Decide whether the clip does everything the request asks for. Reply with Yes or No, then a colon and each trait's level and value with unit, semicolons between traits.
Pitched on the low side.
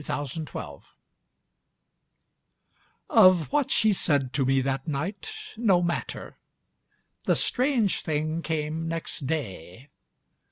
No: medium, 160 Hz